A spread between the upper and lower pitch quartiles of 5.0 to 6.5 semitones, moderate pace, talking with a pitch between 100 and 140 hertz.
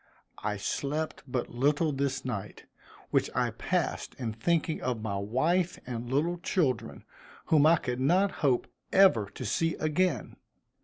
Yes: wide, 5.4 semitones; average, 145 wpm; low, 135 Hz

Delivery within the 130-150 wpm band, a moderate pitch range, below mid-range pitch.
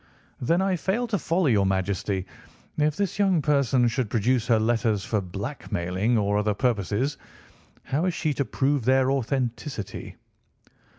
No: average, 145 wpm; wide, 6.0 semitones; low, 125 Hz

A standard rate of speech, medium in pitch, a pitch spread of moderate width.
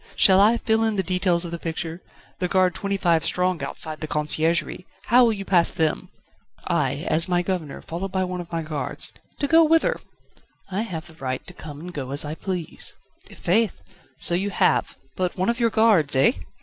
No: fast, 210 wpm; medium, 180 Hz; average, 3.5 semitones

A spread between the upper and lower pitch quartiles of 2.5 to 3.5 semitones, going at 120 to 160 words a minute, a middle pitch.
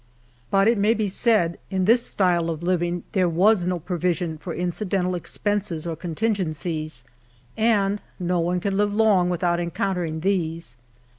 Yes: average, 2.9 semitones; average, 150 wpm; medium, 180 Hz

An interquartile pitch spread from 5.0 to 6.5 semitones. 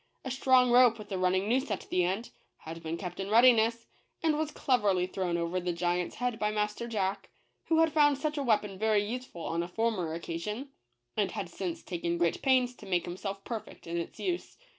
Yes: wide, 5.6 semitones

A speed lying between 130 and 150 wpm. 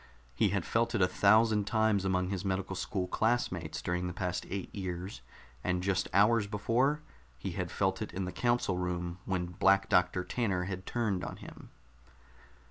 No: average, 175 wpm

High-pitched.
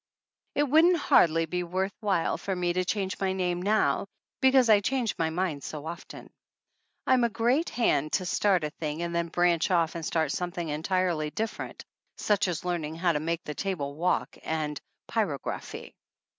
No: medium, 180 Hz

